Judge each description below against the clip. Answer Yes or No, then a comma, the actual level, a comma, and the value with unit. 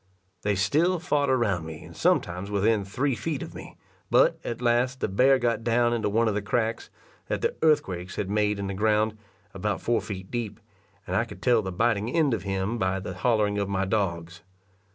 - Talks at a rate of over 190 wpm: Yes, fast, 205 wpm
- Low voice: Yes, low, 110 Hz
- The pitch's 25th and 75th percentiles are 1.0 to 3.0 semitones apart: No, average, 3.7 semitones